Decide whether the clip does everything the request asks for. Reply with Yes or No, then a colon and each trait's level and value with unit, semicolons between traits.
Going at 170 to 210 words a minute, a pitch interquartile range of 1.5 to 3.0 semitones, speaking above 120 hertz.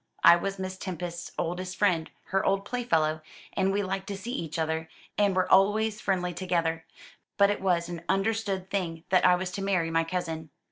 Yes: average, 190 wpm; average, 2.7 semitones; medium, 185 Hz